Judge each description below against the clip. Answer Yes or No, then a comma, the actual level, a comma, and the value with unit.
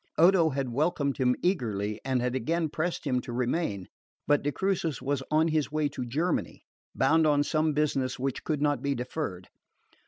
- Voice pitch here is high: No, medium, 145 Hz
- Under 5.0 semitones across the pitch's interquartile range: Yes, average, 3.9 semitones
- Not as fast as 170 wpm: No, average, 175 wpm